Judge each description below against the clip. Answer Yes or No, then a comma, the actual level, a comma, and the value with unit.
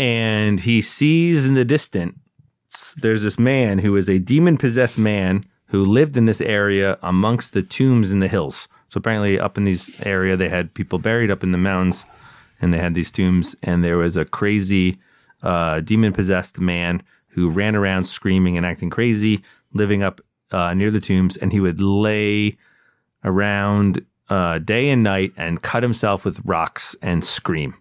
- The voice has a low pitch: Yes, low, 100 Hz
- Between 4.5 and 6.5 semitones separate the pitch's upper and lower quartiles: No, average, 3.0 semitones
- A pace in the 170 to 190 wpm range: Yes, average, 180 wpm